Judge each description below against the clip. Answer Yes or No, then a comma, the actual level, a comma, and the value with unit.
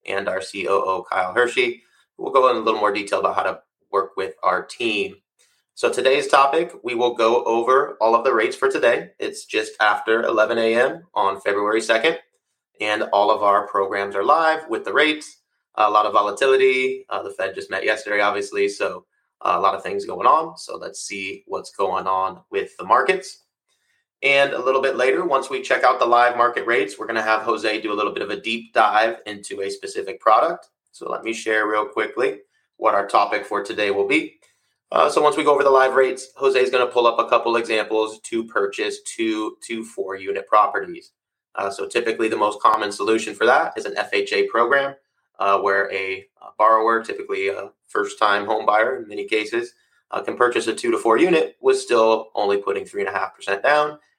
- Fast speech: Yes, fast, 210 wpm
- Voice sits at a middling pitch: Yes, medium, 165 Hz